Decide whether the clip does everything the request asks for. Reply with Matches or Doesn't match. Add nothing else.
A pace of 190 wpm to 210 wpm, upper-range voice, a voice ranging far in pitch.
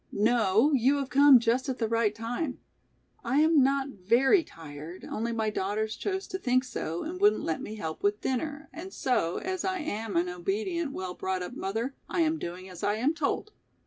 Matches